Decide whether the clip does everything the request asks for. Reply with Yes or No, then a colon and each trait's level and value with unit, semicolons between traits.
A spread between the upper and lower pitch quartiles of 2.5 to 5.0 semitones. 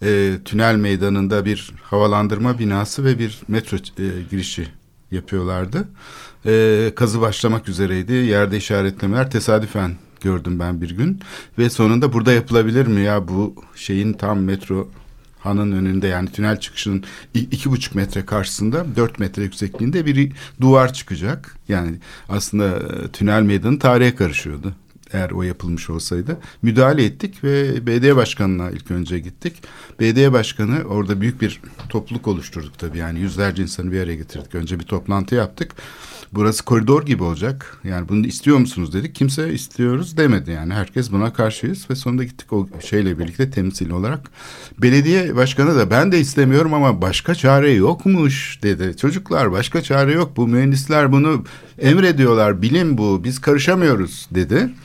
No: wide, 5.4 semitones